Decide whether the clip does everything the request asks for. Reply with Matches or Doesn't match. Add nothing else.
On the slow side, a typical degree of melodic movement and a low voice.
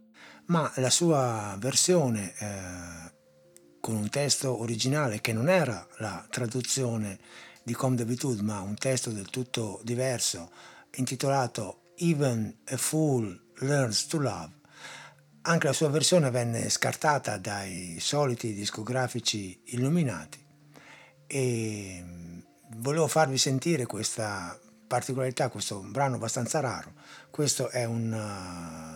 Matches